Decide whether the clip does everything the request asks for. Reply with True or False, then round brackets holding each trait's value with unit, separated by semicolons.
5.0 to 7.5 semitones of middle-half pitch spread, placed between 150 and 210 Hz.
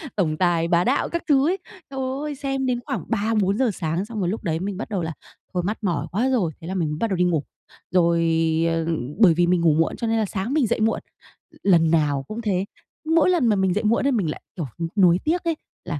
True (5.6 semitones; 190 Hz)